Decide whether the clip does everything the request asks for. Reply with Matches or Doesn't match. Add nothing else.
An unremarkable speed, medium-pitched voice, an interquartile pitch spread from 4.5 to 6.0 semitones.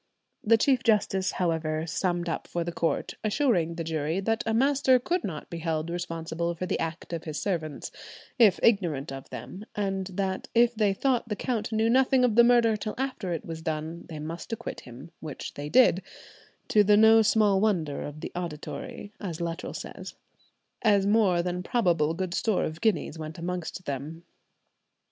Matches